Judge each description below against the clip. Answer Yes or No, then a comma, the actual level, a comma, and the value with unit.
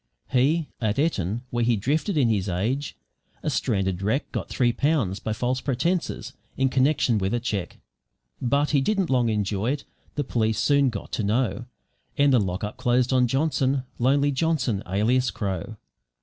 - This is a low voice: Yes, low, 125 Hz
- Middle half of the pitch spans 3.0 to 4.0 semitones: No, average, 4.7 semitones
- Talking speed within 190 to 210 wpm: No, average, 165 wpm